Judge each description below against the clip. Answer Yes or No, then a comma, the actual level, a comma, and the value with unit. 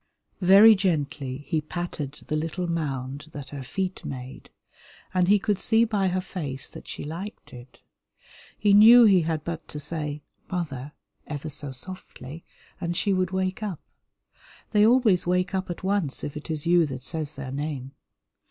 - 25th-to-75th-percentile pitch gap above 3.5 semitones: Yes, average, 4.5 semitones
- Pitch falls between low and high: Yes, medium, 165 Hz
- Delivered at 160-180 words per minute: Yes, average, 170 wpm